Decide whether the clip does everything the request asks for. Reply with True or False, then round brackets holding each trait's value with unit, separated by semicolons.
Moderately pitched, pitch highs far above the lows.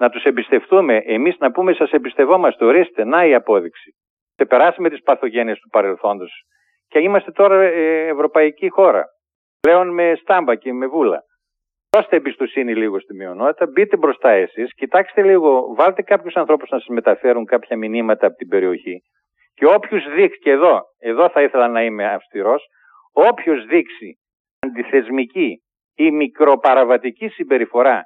True (165 Hz; 7.4 semitones)